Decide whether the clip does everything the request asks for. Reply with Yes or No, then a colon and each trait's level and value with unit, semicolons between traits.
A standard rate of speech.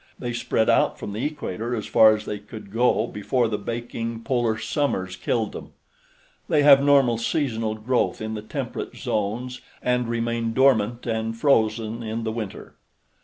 Yes: average, 165 wpm